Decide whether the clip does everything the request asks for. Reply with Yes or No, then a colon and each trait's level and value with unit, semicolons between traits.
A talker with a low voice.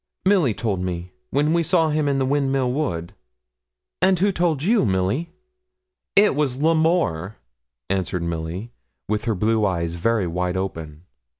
Yes: low, 115 Hz